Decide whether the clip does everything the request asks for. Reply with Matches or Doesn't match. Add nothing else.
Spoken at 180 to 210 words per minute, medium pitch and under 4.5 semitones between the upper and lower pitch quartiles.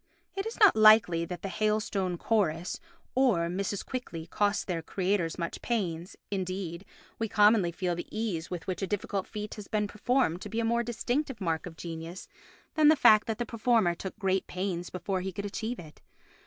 Doesn't match